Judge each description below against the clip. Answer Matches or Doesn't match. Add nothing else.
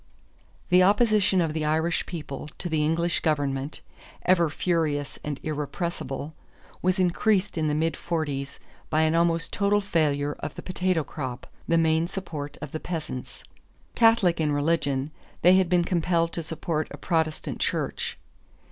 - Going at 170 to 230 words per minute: Doesn't match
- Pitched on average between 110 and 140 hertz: Doesn't match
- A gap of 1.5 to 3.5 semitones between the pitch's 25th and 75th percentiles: Matches